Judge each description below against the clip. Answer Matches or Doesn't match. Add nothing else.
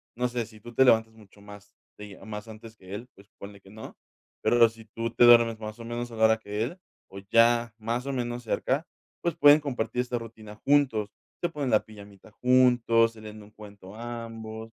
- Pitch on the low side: Matches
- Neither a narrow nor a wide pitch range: Doesn't match